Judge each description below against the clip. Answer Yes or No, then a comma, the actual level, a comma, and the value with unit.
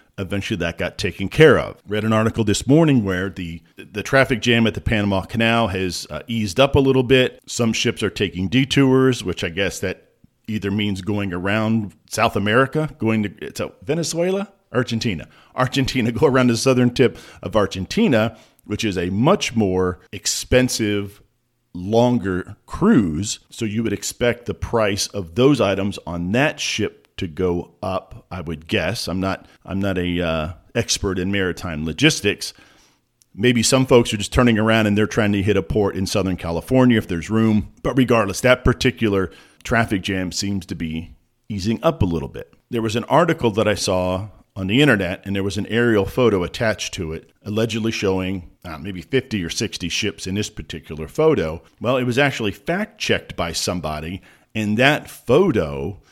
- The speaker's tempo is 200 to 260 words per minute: No, average, 180 wpm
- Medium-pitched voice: No, low, 105 Hz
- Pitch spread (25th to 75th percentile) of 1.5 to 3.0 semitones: No, average, 4.2 semitones